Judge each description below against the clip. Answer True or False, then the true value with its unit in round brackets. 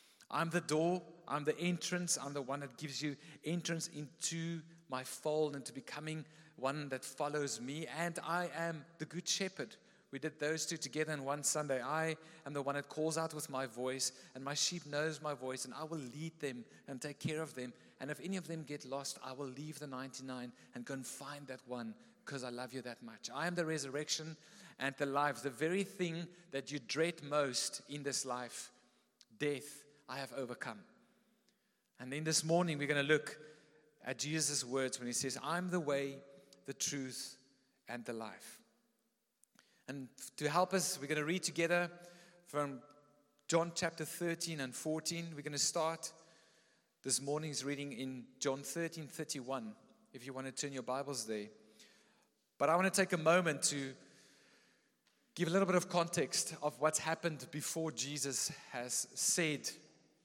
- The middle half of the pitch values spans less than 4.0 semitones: True (3.6 semitones)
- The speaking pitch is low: False (150 Hz)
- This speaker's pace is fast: False (185 wpm)